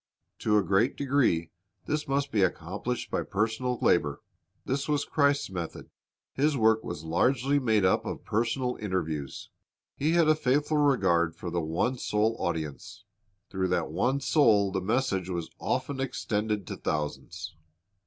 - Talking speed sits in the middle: Yes, average, 150 wpm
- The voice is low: Yes, low, 110 Hz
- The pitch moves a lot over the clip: Yes, wide, 7.2 semitones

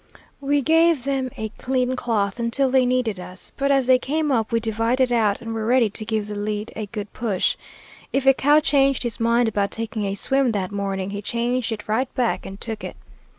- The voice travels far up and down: No, average, 3.7 semitones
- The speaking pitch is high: Yes, high, 235 Hz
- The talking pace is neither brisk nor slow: No, fast, 215 wpm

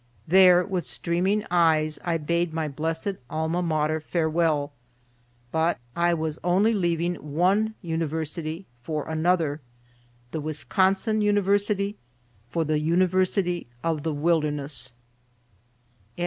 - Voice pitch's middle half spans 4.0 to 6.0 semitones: No, average, 2.8 semitones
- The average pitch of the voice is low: No, medium, 170 Hz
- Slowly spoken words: Yes, slow, 105 wpm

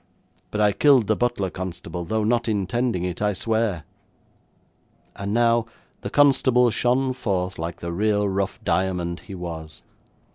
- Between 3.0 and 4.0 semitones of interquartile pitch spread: No, average, 4.5 semitones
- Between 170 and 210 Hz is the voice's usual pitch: No, low, 105 Hz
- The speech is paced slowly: No, average, 145 wpm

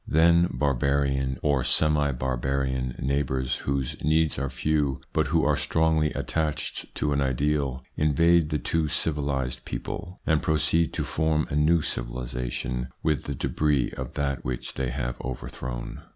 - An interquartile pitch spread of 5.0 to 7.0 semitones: No, average, 3.0 semitones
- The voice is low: Yes, very low, 70 Hz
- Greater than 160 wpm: No, average, 145 wpm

